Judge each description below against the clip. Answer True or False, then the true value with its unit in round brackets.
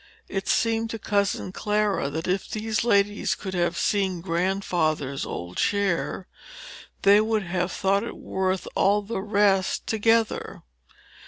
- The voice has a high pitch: True (195 Hz)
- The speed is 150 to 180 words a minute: False (135 wpm)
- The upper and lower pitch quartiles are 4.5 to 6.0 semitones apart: False (2.5 semitones)